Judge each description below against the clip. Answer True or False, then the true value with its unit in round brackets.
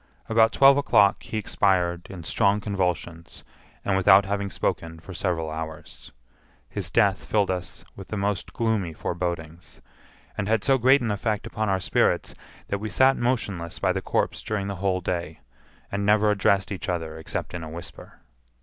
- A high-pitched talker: False (100 Hz)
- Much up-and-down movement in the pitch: False (3.3 semitones)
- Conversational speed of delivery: True (170 wpm)